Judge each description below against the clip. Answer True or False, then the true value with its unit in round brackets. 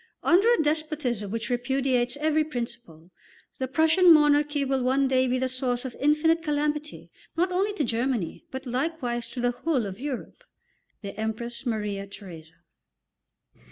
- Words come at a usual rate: True (150 wpm)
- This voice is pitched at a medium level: False (260 Hz)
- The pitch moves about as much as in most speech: True (4.1 semitones)